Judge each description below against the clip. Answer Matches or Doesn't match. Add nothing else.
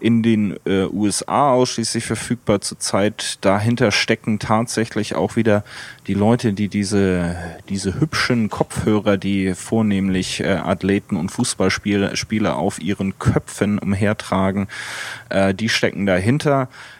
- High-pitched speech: Doesn't match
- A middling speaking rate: Doesn't match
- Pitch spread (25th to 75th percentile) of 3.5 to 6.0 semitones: Doesn't match